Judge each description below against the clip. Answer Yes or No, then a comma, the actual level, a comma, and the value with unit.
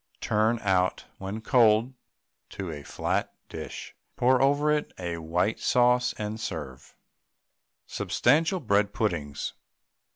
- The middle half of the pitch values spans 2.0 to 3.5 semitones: No, average, 5.1 semitones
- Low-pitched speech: Yes, low, 110 Hz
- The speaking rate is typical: No, slow, 120 wpm